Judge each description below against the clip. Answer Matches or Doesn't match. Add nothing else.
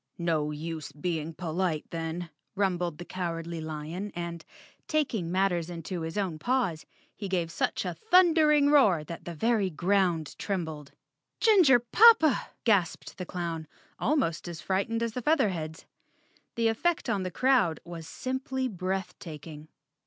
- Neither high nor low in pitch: Matches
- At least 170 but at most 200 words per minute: Doesn't match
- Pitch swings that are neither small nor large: Doesn't match